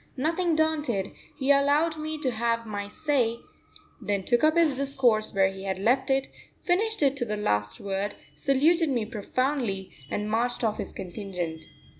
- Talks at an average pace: Yes, average, 165 wpm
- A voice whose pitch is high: Yes, high, 240 Hz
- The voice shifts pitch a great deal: Yes, wide, 6.3 semitones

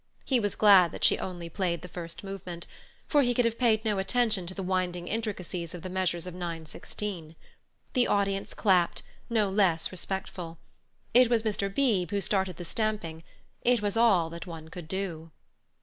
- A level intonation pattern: No, average, 3.6 semitones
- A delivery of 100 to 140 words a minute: No, average, 180 wpm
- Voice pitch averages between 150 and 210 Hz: Yes, high, 190 Hz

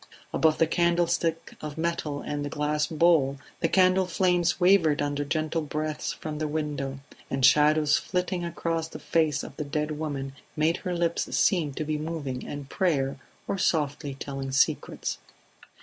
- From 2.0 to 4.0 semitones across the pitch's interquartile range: Yes, narrow, 2.6 semitones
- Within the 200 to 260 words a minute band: No, average, 160 wpm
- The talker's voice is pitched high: No, medium, 155 Hz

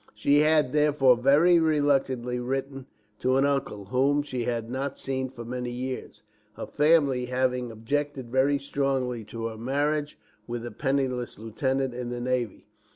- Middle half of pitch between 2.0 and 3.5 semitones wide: Yes, narrow, 2.6 semitones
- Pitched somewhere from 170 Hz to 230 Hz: No, low, 130 Hz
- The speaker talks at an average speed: Yes, average, 155 wpm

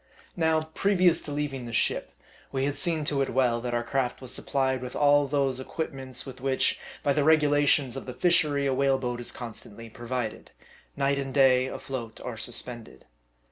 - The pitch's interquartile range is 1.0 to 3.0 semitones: Yes, narrow, 2.6 semitones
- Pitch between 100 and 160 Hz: Yes, low, 135 Hz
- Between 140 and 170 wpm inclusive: No, average, 180 wpm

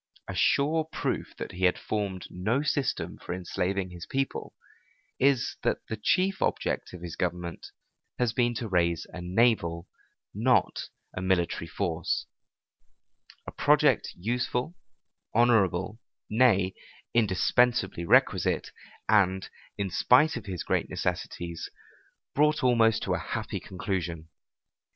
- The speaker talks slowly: Yes, slow, 125 wpm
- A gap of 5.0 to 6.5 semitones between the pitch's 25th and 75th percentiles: Yes, wide, 5.5 semitones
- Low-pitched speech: Yes, low, 100 Hz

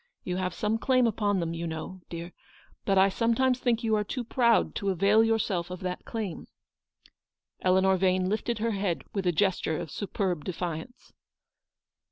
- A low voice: No, high, 195 Hz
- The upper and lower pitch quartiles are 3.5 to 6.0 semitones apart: Yes, average, 3.8 semitones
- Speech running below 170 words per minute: No, average, 175 wpm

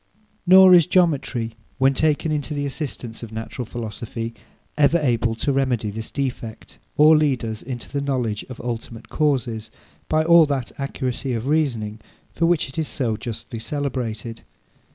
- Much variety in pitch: No, average, 4.5 semitones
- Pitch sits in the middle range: No, low, 130 Hz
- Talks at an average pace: Yes, average, 155 wpm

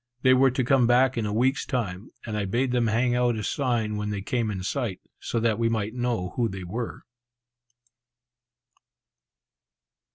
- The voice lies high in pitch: No, low, 115 Hz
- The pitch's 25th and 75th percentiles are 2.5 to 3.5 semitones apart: Yes, average, 2.9 semitones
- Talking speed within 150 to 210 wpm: Yes, average, 175 wpm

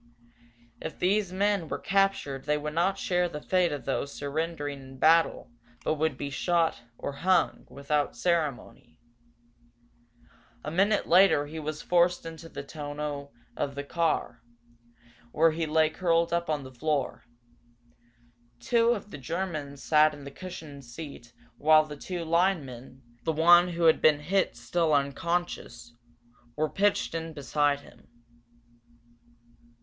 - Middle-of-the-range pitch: Yes, medium, 155 Hz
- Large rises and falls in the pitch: No, average, 3.3 semitones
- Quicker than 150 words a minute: No, average, 140 wpm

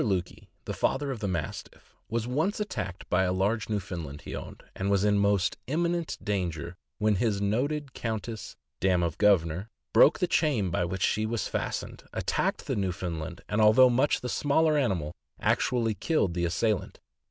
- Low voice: Yes, low, 105 Hz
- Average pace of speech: Yes, average, 170 wpm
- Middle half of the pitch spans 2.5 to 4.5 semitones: No, wide, 5.4 semitones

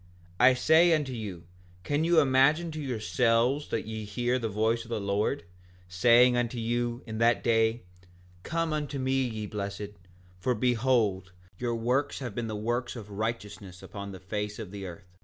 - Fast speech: No, average, 175 wpm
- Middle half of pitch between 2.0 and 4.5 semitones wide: Yes, average, 3.7 semitones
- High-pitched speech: No, low, 115 Hz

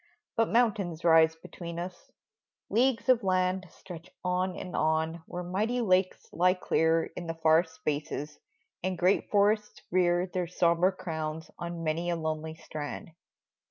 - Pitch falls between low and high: Yes, medium, 175 Hz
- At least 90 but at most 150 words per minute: Yes, average, 145 wpm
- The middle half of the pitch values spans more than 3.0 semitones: No, narrow, 2.5 semitones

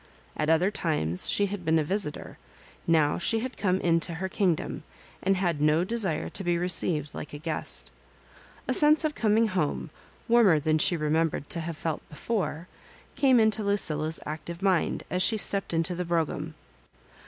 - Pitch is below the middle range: No, medium, 170 Hz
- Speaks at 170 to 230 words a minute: Yes, average, 175 wpm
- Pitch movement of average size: Yes, average, 4.2 semitones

